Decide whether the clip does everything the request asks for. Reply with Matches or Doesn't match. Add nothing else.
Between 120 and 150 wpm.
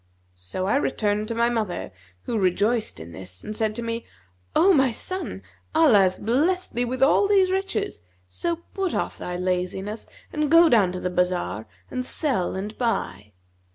Doesn't match